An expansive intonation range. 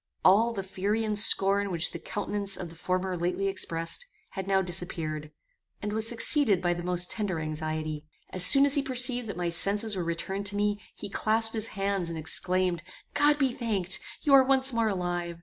No: average, 3.9 semitones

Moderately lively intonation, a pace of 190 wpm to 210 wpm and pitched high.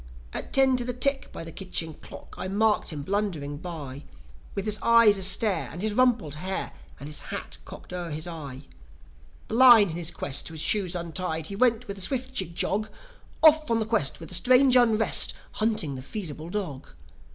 No: wide, 5.8 semitones; average, 195 wpm; high, 195 Hz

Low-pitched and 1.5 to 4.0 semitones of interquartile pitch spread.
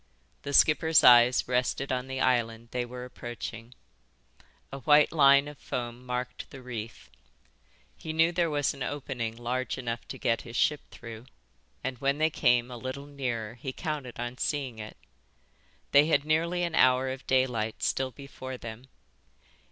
Yes: low, 130 Hz; average, 2.9 semitones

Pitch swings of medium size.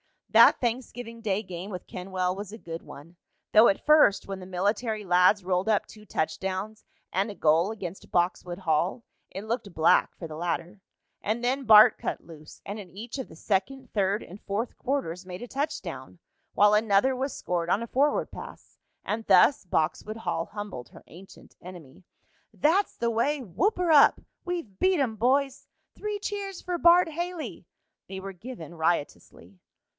No: wide, 5.7 semitones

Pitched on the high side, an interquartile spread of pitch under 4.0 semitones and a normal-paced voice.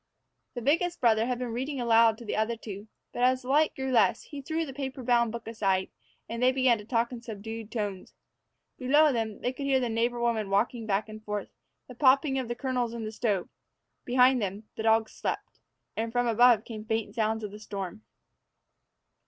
No: high, 235 Hz; average, 2.7 semitones; fast, 210 wpm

